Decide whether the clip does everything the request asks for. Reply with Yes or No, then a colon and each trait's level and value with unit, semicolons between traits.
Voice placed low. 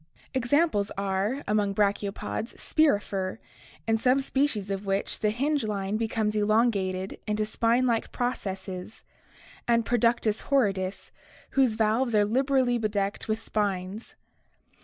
No: high, 215 Hz